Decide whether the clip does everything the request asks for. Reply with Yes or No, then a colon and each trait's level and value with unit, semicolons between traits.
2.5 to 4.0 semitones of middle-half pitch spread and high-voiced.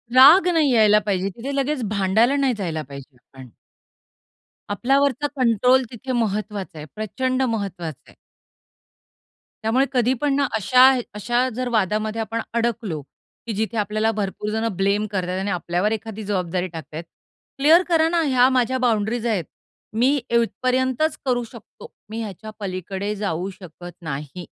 No: average, 4.8 semitones; high, 220 Hz